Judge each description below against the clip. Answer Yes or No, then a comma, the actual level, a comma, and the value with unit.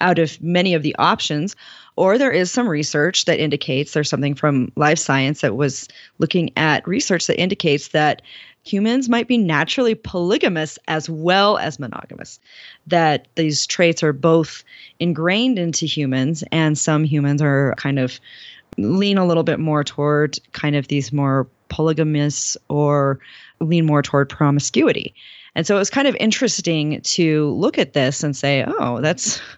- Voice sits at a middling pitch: Yes, medium, 155 Hz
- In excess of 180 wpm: No, average, 160 wpm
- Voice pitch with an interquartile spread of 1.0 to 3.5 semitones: Yes, average, 3.1 semitones